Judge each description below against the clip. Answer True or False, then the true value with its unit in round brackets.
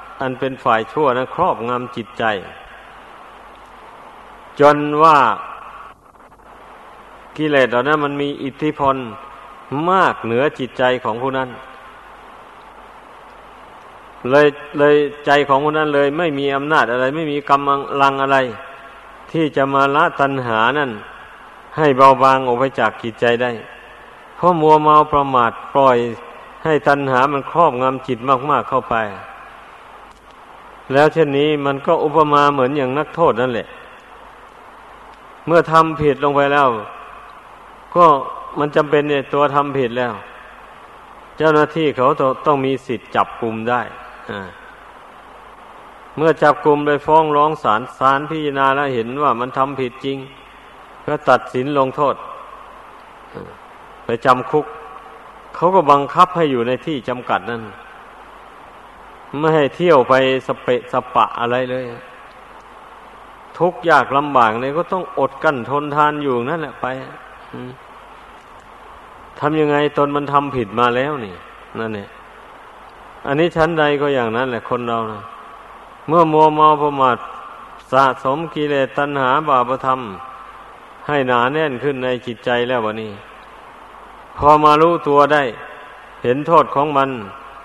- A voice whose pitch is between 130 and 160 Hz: True (140 Hz)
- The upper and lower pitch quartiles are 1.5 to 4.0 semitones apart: True (2.7 semitones)